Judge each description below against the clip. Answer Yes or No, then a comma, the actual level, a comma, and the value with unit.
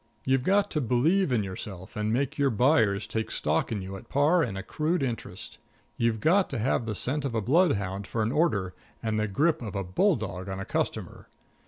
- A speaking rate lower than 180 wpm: No, fast, 205 wpm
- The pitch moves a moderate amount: No, wide, 6.8 semitones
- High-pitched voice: No, low, 115 Hz